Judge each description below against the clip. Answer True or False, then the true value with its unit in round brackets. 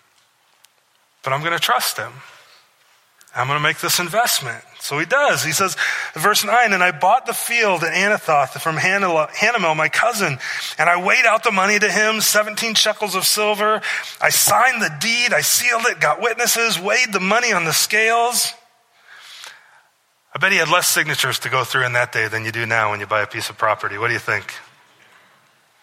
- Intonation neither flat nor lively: False (6.8 semitones)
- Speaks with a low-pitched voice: False (190 Hz)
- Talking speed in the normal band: True (195 wpm)